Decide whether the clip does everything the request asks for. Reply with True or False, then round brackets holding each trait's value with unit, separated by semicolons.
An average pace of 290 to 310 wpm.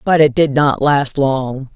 False (205 wpm)